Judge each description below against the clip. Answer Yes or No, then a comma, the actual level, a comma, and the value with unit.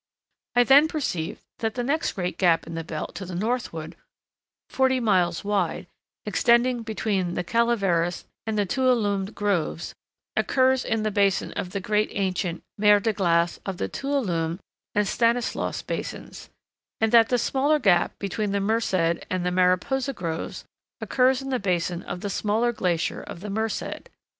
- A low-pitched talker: No, high, 205 Hz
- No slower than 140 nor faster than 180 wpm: Yes, average, 155 wpm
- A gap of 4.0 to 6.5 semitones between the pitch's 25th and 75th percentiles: Yes, average, 4.9 semitones